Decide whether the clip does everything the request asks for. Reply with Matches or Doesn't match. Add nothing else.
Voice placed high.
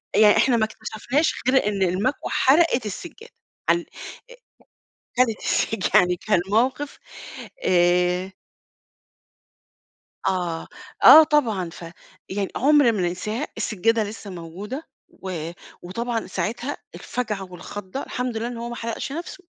Matches